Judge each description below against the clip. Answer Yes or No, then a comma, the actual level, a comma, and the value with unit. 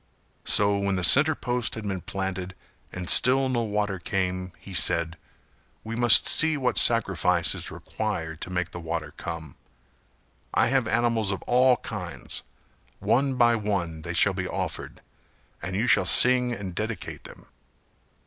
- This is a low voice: Yes, low, 100 Hz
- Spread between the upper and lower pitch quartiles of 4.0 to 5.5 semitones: Yes, average, 4.9 semitones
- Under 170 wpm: Yes, average, 155 wpm